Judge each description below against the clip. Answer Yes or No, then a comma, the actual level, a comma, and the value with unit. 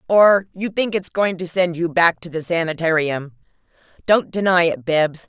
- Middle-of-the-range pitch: Yes, medium, 175 Hz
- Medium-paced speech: Yes, average, 180 wpm